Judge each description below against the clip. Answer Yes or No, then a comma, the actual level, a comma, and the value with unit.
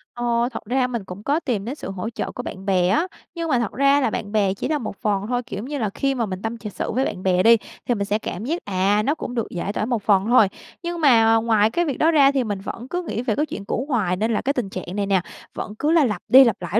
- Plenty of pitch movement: No, average, 4.8 semitones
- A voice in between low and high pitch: No, high, 230 Hz